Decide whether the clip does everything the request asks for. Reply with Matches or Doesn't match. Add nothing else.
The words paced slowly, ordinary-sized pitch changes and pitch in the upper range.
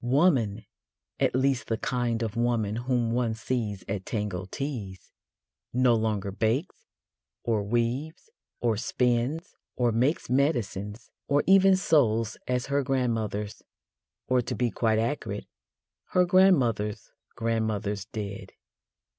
Doesn't match